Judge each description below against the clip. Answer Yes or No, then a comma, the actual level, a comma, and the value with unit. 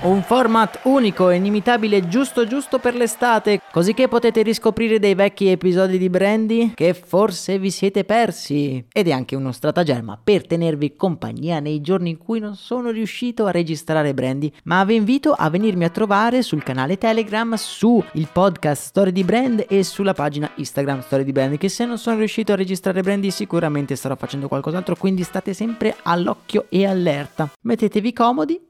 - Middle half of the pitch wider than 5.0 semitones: Yes, wide, 5.5 semitones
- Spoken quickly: Yes, fast, 175 wpm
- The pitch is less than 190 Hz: No, high, 195 Hz